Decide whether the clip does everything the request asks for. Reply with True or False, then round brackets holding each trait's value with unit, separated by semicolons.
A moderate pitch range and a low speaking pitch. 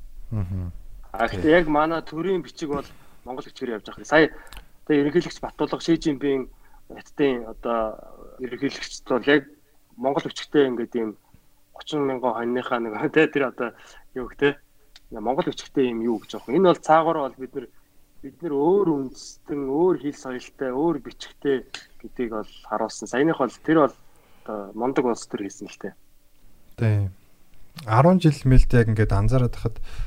True (4.8 semitones; 130 Hz)